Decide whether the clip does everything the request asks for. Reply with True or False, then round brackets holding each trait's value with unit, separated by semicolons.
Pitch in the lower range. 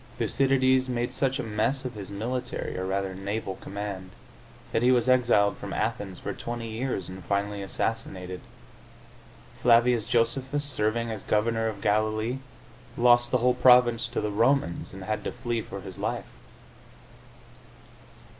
True (115 Hz)